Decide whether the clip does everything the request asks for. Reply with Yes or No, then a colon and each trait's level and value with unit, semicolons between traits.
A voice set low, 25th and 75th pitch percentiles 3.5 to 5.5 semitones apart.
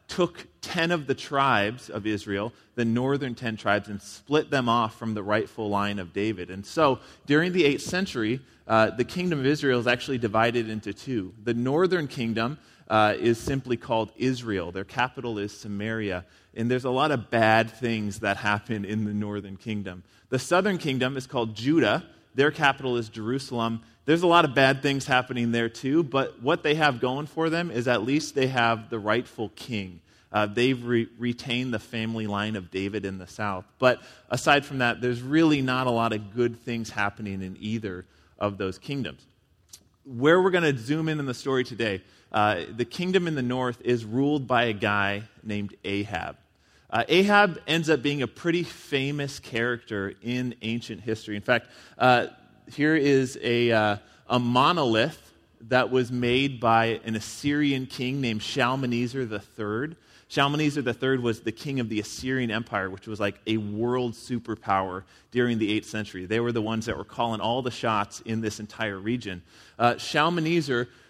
Yes: low, 120 Hz; average, 3.9 semitones